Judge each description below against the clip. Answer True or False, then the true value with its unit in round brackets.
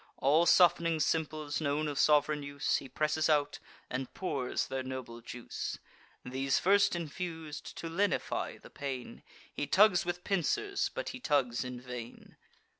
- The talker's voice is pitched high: False (150 Hz)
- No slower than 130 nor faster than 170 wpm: True (145 wpm)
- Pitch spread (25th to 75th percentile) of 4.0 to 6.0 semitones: True (4.3 semitones)